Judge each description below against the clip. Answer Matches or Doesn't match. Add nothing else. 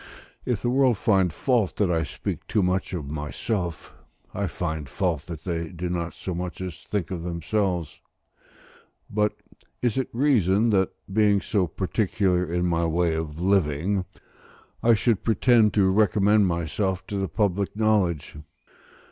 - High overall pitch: Doesn't match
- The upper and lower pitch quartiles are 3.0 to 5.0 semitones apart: Matches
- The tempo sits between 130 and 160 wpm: Matches